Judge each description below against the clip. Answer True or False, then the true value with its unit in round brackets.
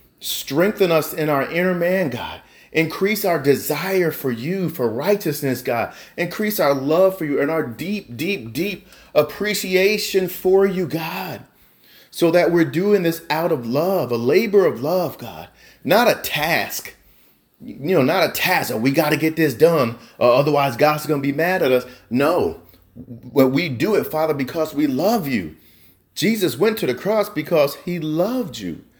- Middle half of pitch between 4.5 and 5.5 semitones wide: True (5.1 semitones)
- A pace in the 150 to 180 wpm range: True (175 wpm)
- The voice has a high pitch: False (160 Hz)